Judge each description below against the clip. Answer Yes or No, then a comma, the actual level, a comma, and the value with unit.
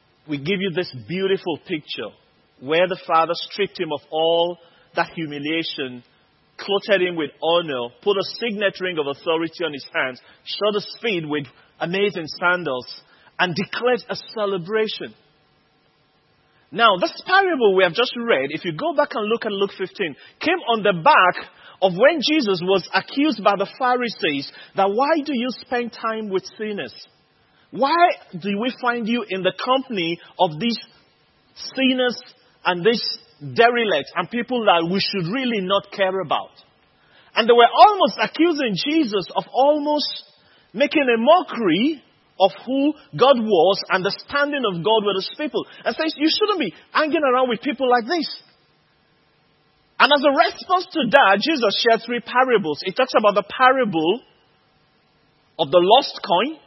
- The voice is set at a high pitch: Yes, high, 210 Hz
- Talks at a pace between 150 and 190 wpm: Yes, average, 160 wpm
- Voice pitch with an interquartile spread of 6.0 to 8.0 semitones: Yes, wide, 6.3 semitones